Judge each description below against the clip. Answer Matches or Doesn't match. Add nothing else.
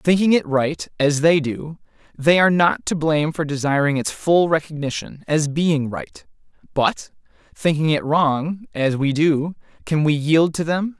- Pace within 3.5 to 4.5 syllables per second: Matches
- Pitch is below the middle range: Doesn't match